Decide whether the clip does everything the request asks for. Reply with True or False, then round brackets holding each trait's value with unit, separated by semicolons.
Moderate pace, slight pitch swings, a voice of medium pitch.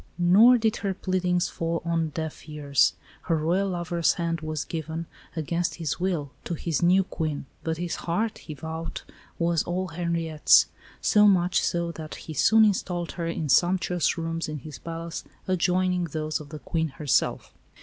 True (165 wpm; 2.0 semitones; 170 Hz)